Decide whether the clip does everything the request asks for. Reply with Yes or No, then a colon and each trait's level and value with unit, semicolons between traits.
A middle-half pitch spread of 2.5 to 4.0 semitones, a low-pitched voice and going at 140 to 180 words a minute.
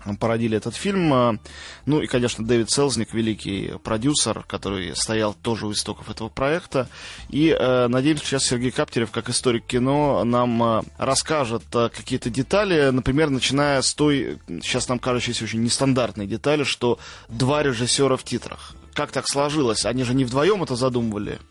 Yes: average, 3.3 semitones; low, 125 Hz; average, 150 wpm